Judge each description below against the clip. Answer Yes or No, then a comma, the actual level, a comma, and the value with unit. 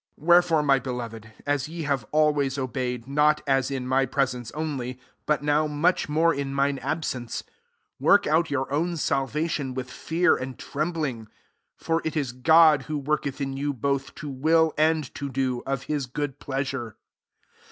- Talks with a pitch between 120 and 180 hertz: Yes, medium, 140 Hz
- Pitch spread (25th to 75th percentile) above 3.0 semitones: No, average, 2.7 semitones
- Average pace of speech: Yes, average, 175 wpm